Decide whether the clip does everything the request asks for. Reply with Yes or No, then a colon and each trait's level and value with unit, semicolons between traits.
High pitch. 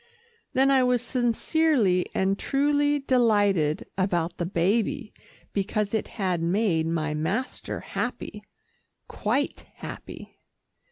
Yes: high, 210 Hz